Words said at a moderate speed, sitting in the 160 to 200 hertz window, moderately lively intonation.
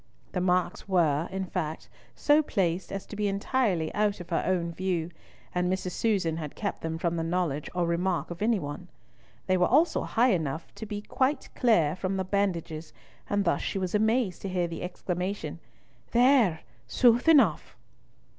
Yes: average, 180 wpm; medium, 185 Hz; average, 3.6 semitones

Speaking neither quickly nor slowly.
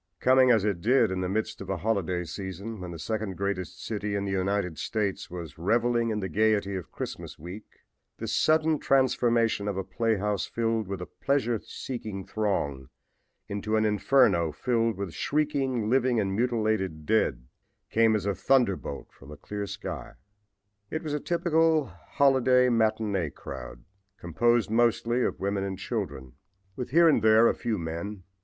Yes: average, 165 wpm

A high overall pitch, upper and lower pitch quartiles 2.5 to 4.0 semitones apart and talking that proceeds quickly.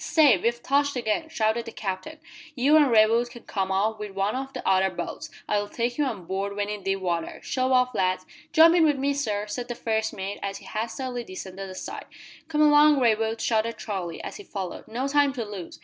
No: high, 225 Hz; average, 5.0 semitones; fast, 220 wpm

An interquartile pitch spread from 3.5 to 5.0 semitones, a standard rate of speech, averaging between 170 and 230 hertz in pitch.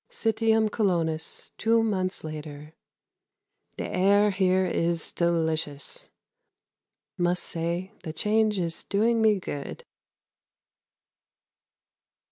No: average, 4.5 semitones; slow, 90 wpm; medium, 185 Hz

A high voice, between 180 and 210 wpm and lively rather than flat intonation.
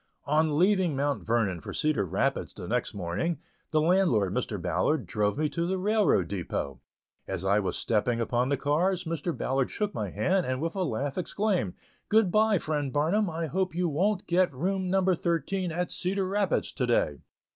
No: medium, 160 Hz; average, 185 wpm; wide, 7.1 semitones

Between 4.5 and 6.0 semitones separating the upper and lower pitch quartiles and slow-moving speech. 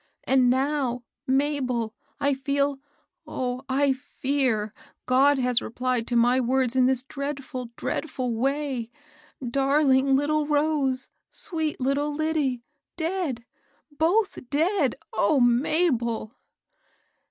No: average, 2.7 semitones; slow, 115 wpm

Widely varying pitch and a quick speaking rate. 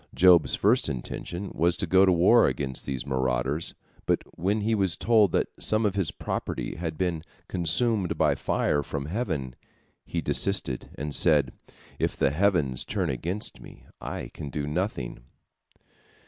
No: wide, 5.7 semitones; average, 155 wpm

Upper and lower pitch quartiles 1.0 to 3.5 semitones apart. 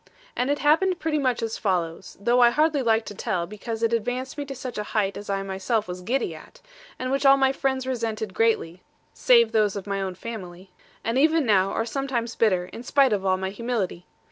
No: average, 5.3 semitones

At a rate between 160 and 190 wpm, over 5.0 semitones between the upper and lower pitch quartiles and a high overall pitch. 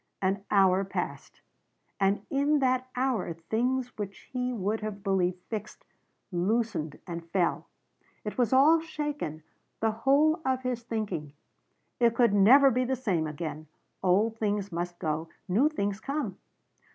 No: average, 140 wpm; wide, 5.6 semitones; high, 215 Hz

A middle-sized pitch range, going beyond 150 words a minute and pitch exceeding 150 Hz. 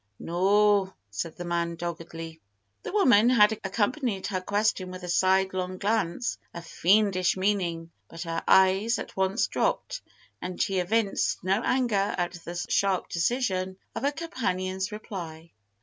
No: average, 3.2 semitones; average, 140 wpm; high, 190 Hz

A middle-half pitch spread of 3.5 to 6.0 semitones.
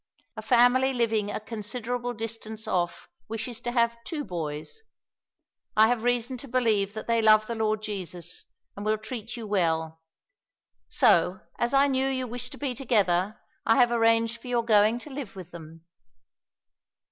No: average, 3.0 semitones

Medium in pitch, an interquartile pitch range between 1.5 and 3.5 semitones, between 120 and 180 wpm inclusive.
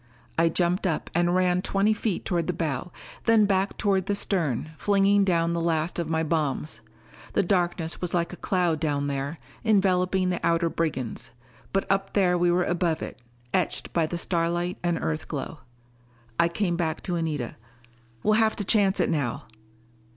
Yes: medium, 175 Hz; average, 2.7 semitones; average, 175 wpm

